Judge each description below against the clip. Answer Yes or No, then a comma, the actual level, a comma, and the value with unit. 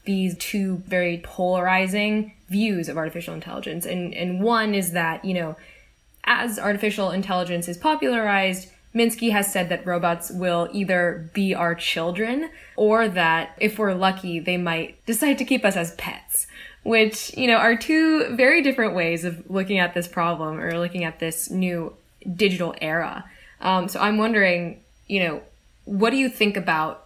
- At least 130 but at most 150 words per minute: No, average, 165 wpm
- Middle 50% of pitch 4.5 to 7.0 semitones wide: No, average, 3.7 semitones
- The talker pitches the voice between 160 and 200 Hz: Yes, medium, 185 Hz